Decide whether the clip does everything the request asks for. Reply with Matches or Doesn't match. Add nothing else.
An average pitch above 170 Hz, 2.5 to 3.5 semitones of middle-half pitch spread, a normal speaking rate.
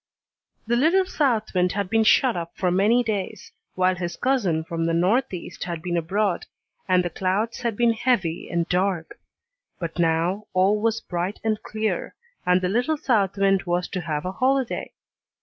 Doesn't match